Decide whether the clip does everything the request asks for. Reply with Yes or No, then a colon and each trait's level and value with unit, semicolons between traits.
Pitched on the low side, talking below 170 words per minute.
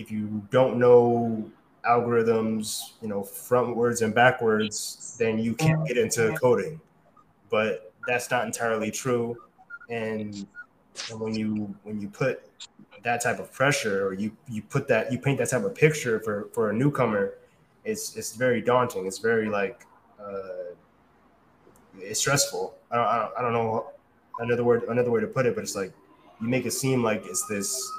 No: low, 120 Hz; average, 175 wpm